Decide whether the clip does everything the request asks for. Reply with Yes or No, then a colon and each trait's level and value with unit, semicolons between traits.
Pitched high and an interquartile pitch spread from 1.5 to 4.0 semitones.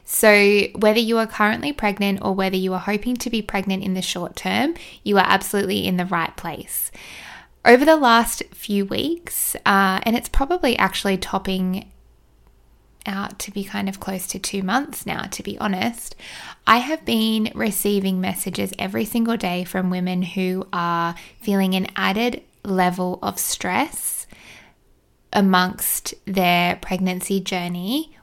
Yes: high, 200 Hz; average, 3.3 semitones